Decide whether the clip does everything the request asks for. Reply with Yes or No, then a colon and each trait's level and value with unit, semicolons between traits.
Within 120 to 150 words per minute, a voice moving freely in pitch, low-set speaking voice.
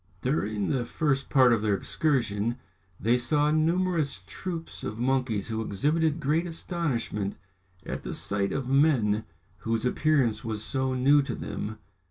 Yes: average, 145 wpm; wide, 5.7 semitones; low, 130 Hz